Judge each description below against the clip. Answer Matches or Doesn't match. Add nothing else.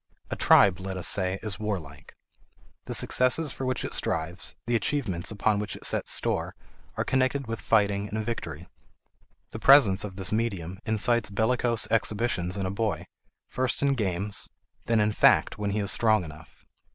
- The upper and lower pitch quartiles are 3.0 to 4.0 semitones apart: Matches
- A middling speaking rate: Matches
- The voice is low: Matches